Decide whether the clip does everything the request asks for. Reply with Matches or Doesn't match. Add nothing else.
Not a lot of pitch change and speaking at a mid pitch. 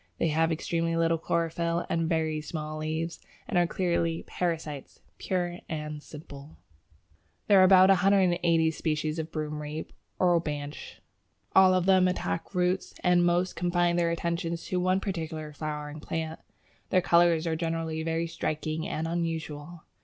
Matches